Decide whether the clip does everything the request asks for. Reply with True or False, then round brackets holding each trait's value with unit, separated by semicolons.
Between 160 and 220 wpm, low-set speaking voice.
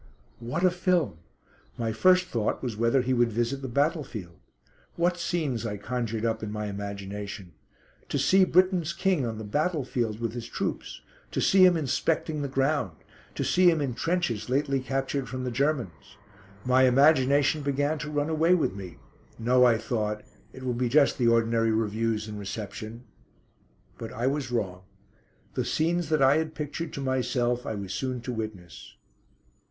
True (170 wpm; 125 Hz)